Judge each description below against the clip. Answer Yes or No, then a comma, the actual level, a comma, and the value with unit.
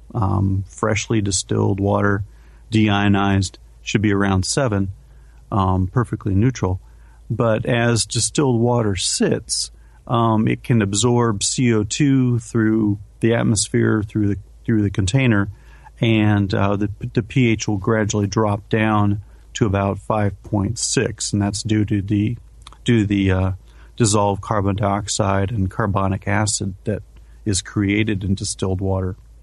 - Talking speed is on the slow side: Yes, slow, 130 wpm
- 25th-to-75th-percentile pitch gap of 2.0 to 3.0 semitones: Yes, narrow, 2.4 semitones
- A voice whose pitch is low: Yes, low, 105 Hz